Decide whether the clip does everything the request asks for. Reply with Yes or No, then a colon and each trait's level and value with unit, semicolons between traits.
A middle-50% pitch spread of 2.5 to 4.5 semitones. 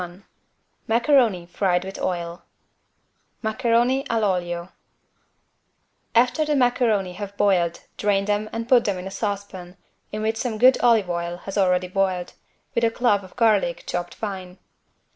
Yes: average, 4.1 semitones